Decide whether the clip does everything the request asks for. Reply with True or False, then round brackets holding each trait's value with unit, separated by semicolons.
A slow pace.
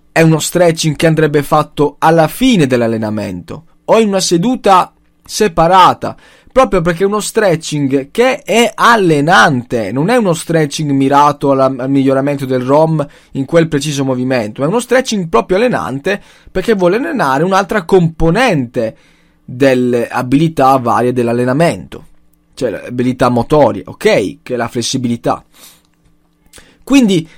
False (130 wpm)